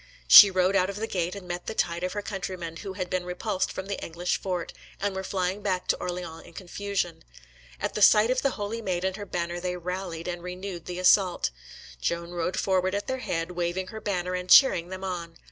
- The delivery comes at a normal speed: No, fast, 225 wpm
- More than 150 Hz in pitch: Yes, medium, 185 Hz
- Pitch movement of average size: No, narrow, 2.0 semitones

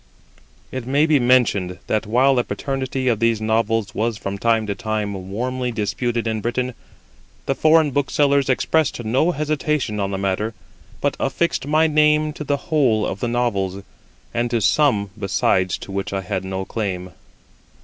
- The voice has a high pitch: No, low, 115 Hz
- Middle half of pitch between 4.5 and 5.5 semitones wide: Yes, average, 5.1 semitones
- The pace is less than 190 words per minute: Yes, average, 165 wpm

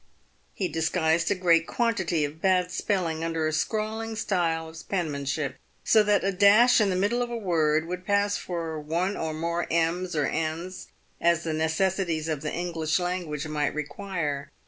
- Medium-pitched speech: Yes, medium, 170 Hz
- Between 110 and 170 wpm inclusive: No, average, 180 wpm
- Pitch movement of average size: Yes, average, 3.3 semitones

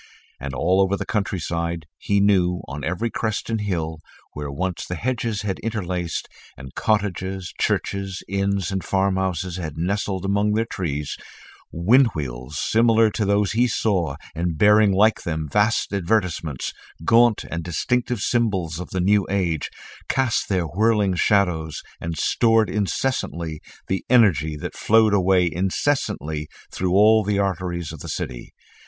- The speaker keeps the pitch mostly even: No, average, 3.9 semitones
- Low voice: Yes, very low, 95 Hz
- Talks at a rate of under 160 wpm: Yes, average, 150 wpm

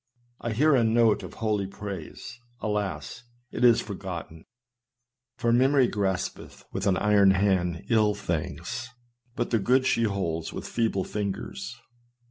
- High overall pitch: No, low, 105 Hz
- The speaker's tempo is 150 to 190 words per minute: No, slow, 135 wpm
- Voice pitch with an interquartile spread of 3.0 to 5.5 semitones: Yes, average, 3.6 semitones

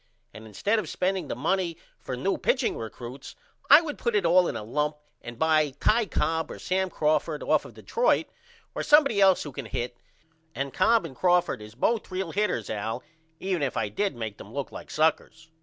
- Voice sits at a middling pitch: Yes, medium, 160 Hz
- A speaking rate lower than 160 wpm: No, average, 200 wpm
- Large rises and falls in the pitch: Yes, wide, 7.1 semitones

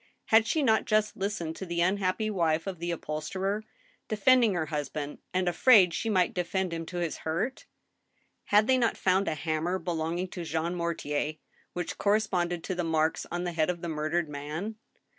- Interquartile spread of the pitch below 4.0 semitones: Yes, average, 3.6 semitones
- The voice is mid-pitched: Yes, medium, 175 Hz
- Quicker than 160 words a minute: Yes, average, 180 wpm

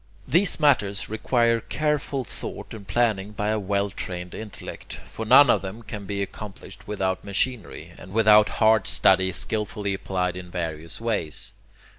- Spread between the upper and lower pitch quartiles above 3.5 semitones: No, average, 3.1 semitones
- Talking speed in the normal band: Yes, average, 150 wpm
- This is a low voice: Yes, low, 105 Hz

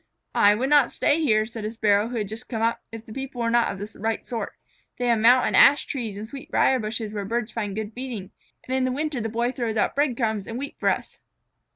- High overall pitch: Yes, high, 230 Hz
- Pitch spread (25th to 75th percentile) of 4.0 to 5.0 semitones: No, average, 2.9 semitones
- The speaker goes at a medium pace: No, fast, 255 wpm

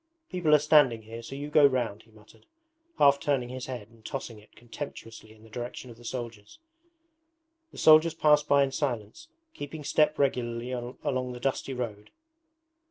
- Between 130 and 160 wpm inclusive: No, average, 170 wpm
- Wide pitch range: No, average, 3.8 semitones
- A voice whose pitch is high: No, low, 125 Hz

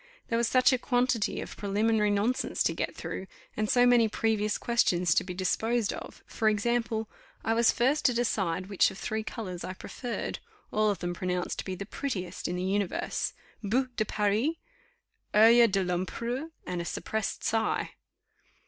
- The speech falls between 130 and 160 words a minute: No, average, 175 wpm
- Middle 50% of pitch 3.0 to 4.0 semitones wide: Yes, average, 3.7 semitones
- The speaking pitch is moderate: No, high, 215 Hz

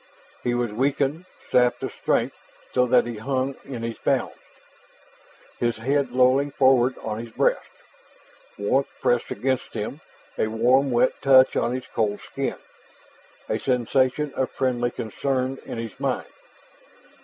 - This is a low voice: Yes, low, 125 Hz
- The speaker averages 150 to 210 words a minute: No, average, 140 wpm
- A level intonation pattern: Yes, narrow, 2.1 semitones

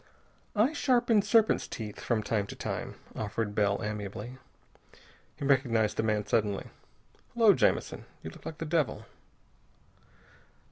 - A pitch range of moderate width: No, wide, 7.7 semitones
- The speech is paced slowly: Yes, slow, 130 wpm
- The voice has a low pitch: Yes, low, 115 Hz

